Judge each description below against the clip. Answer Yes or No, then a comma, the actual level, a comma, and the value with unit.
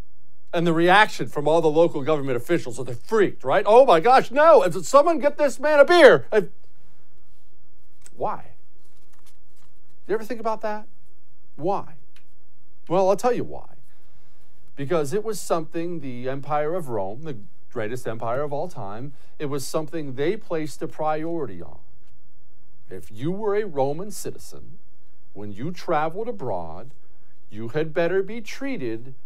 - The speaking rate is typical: Yes, average, 155 wpm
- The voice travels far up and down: Yes, wide, 7.0 semitones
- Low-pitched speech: No, medium, 155 Hz